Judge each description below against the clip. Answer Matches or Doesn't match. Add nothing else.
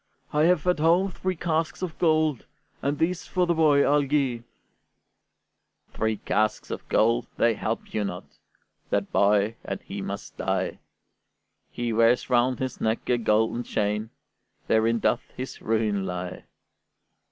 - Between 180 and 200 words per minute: Doesn't match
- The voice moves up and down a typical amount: Doesn't match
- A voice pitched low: Matches